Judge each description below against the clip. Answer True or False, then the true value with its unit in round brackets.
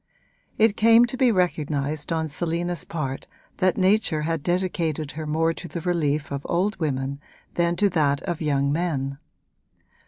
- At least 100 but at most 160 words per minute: True (155 wpm)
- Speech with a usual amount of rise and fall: True (3.4 semitones)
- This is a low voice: False (165 Hz)